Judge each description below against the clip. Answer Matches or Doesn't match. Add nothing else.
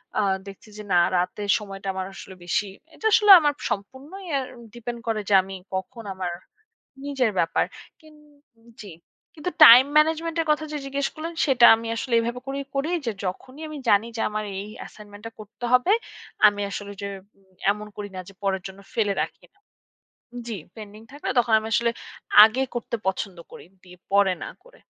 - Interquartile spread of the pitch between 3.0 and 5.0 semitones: Doesn't match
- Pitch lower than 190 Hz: Doesn't match